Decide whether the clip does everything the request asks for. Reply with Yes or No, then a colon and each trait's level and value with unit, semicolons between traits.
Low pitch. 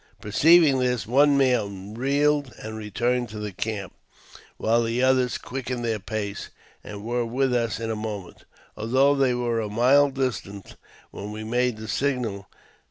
Yes: low, 120 Hz